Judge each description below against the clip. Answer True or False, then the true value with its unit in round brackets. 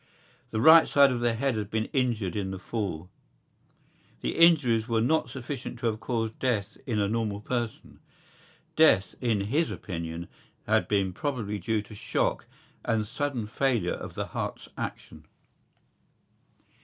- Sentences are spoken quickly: False (150 wpm)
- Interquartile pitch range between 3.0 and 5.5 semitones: True (3.6 semitones)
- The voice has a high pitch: False (115 Hz)